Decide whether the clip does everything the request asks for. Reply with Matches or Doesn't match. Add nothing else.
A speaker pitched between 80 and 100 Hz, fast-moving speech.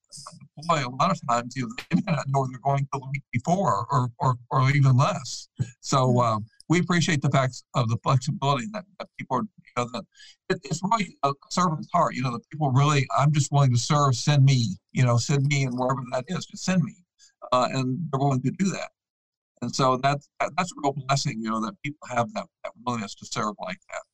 Doesn't match